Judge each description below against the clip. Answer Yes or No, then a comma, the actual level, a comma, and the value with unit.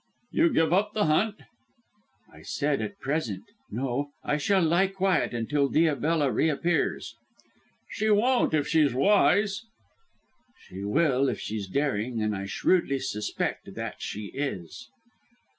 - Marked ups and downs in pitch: Yes, wide, 7.0 semitones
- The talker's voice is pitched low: No, medium, 150 Hz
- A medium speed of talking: No, slow, 130 wpm